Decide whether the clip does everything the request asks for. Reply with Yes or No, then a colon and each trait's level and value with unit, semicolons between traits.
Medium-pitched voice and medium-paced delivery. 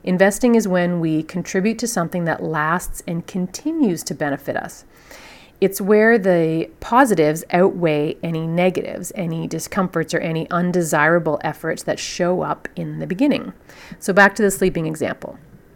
Yes: medium, 175 Hz; average, 150 wpm